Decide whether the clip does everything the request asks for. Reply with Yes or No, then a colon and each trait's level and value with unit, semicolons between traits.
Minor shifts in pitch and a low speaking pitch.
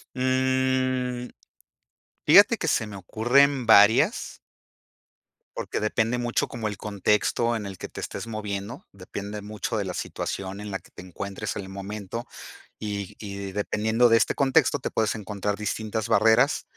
No: average, 3.1 semitones; low, 105 Hz